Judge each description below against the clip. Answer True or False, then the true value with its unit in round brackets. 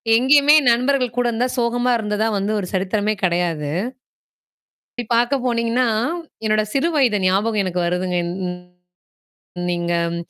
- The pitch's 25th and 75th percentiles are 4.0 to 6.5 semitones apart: True (4.8 semitones)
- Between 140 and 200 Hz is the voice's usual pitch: False (220 Hz)